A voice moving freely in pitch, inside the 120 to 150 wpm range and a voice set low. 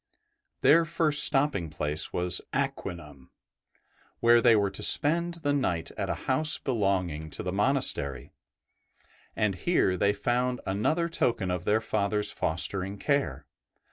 Yes: wide, 7.5 semitones; slow, 135 wpm; low, 105 Hz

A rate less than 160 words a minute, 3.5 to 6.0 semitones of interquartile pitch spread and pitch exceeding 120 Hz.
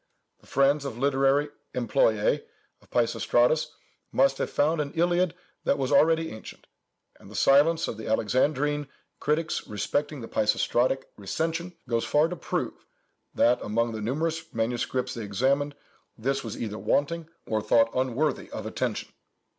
Yes: average, 145 wpm; average, 5.2 semitones; medium, 140 Hz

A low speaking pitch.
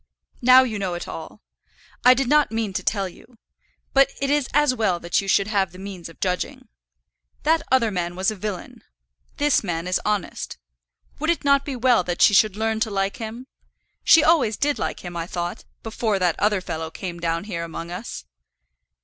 No: high, 205 Hz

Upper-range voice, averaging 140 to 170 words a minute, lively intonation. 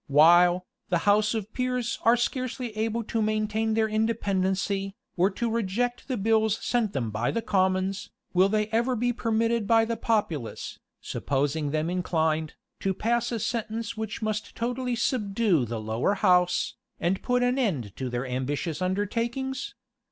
No: high, 210 Hz; average, 155 wpm; average, 4.4 semitones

